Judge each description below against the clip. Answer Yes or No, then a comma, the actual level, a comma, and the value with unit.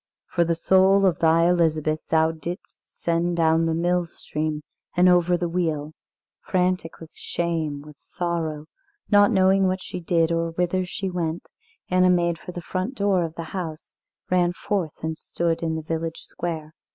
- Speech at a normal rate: Yes, average, 170 wpm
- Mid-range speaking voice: Yes, medium, 170 Hz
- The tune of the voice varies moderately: No, narrow, 1.9 semitones